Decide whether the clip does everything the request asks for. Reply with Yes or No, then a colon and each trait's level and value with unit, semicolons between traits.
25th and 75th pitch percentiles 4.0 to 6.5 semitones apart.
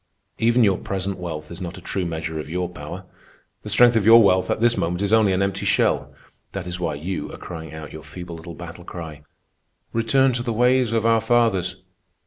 Yes: average, 4.9 semitones